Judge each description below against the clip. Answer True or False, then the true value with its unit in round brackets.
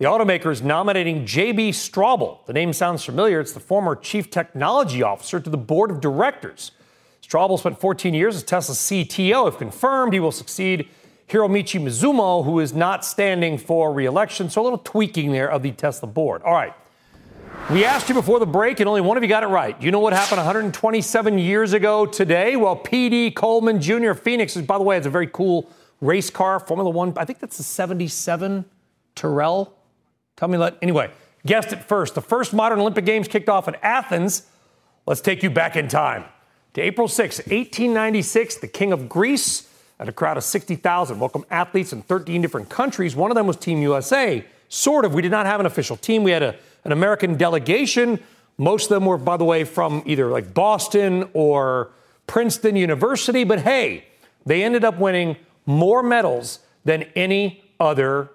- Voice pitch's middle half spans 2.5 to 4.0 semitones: False (4.6 semitones)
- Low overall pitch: False (185 Hz)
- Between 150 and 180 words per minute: False (190 wpm)